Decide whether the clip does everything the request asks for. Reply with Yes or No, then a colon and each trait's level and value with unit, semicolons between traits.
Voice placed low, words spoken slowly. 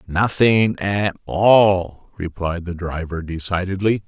Yes: very low, 95 Hz; slow, 105 wpm